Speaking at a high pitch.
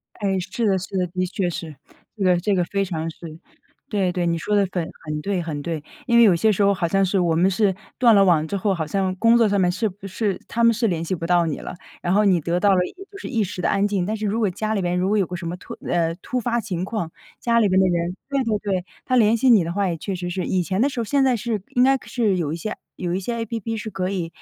Yes: high, 195 Hz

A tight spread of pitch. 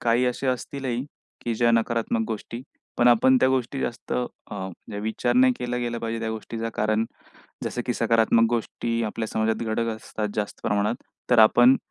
Yes: narrow, 1.7 semitones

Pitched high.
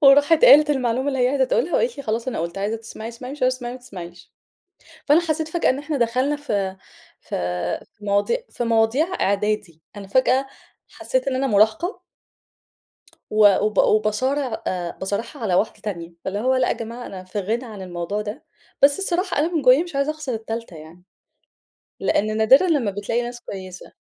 Yes: high, 235 Hz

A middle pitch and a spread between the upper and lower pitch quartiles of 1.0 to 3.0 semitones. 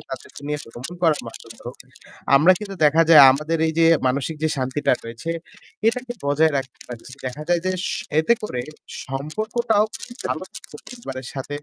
No: medium, 150 Hz; average, 4.9 semitones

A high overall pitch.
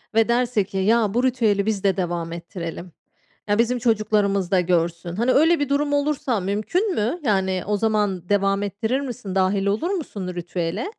Yes: high, 205 Hz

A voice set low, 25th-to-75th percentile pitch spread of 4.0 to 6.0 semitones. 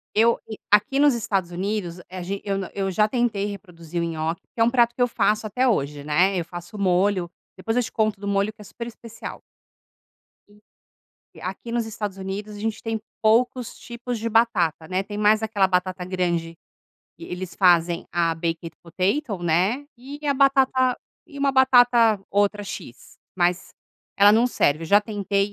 No: high, 205 Hz; average, 4.4 semitones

